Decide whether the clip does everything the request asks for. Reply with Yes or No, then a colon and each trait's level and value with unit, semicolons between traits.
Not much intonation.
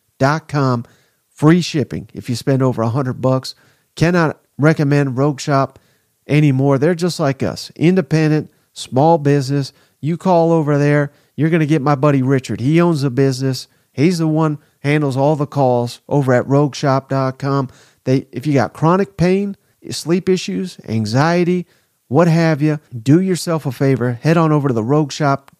No: average, 3.2 semitones